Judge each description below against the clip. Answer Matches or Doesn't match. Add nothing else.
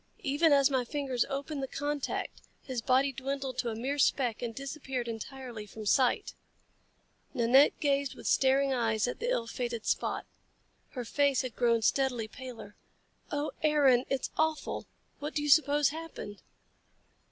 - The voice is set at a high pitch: Matches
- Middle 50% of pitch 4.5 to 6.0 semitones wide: Doesn't match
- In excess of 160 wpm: Doesn't match